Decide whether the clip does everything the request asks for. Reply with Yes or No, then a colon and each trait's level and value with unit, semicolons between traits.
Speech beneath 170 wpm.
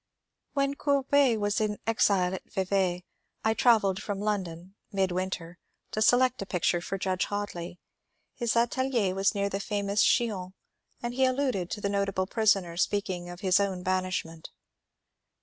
Yes: average, 150 wpm